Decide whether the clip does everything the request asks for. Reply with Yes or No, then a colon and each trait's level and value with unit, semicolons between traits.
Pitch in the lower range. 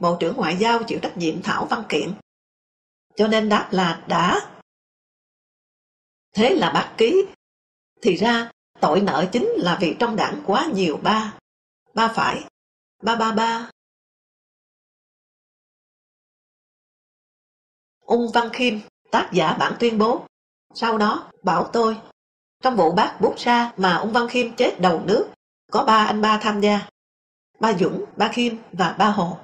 No: high, 225 Hz